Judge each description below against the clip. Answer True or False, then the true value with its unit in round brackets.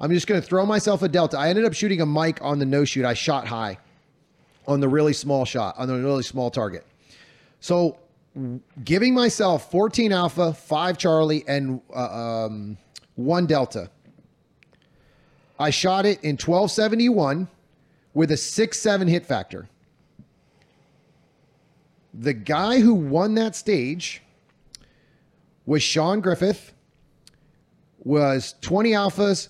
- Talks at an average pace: False (130 wpm)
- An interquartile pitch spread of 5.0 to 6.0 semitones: True (5.5 semitones)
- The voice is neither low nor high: True (160 Hz)